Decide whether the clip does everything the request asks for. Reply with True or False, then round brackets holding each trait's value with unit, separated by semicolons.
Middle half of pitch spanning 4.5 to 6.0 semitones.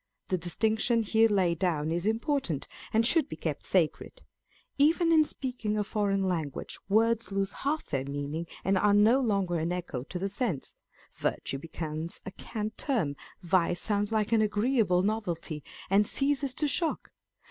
True (4.9 semitones)